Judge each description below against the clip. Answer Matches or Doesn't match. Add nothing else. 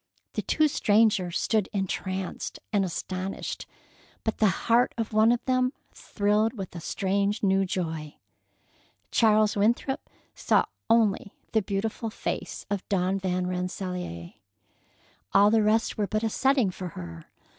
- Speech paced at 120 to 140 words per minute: Matches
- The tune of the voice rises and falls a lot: Doesn't match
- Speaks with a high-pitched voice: Matches